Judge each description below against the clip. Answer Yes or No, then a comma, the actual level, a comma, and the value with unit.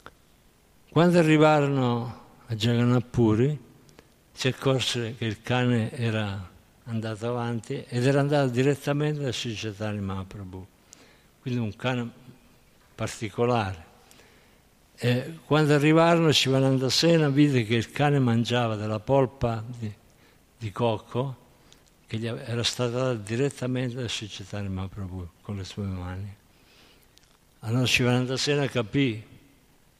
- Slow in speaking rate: Yes, slow, 110 wpm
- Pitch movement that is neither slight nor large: Yes, average, 3.5 semitones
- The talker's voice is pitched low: Yes, low, 120 Hz